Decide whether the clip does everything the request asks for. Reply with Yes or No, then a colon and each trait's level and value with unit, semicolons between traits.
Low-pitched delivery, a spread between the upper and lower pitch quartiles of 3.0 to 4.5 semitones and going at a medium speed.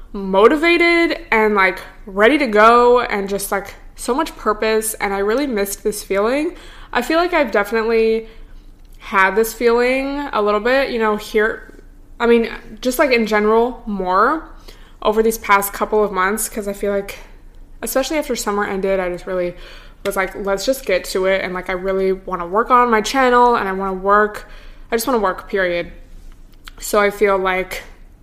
No: high, 215 Hz; average, 3.6 semitones; average, 185 wpm